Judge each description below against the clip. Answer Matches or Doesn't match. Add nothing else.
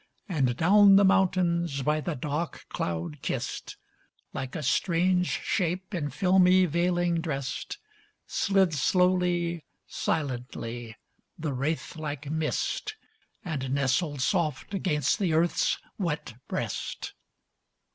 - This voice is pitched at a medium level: Matches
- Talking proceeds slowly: Matches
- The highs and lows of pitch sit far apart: Doesn't match